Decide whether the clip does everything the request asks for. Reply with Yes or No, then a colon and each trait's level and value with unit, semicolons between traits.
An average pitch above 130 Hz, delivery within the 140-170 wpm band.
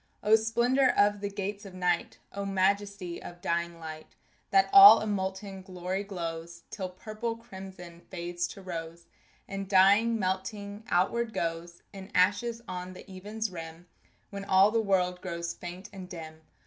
Yes: high, 190 Hz; average, 155 wpm